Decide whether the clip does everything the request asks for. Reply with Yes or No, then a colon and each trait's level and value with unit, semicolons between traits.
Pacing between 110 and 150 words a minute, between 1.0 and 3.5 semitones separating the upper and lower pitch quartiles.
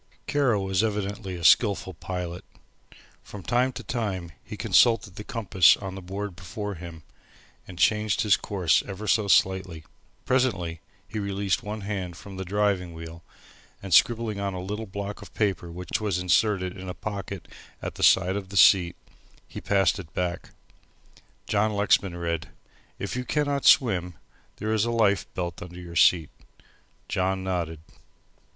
No: average, 160 wpm; average, 2.8 semitones